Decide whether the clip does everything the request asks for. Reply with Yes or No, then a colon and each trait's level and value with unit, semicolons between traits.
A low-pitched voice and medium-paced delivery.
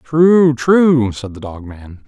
Yes: low, 130 Hz; average, 175 wpm